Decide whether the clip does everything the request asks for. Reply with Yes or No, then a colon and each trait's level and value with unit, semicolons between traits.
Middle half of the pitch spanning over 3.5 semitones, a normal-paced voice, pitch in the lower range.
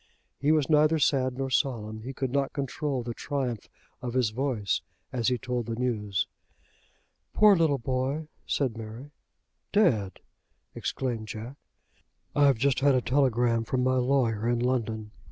No: average, 3.2 semitones; average, 150 wpm; low, 125 Hz